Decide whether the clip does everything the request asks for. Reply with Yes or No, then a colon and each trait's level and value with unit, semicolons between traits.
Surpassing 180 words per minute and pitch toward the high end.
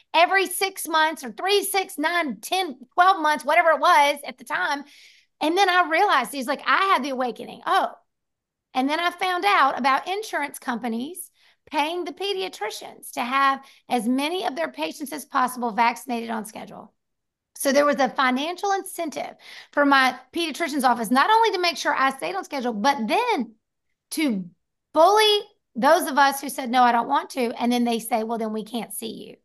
Yes: average, 190 wpm; very high, 290 Hz